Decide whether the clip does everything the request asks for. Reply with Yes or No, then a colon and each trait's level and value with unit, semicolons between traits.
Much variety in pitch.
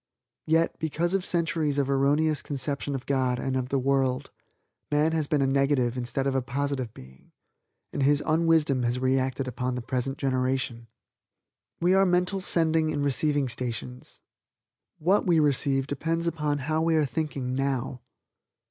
No: average, 3.4 semitones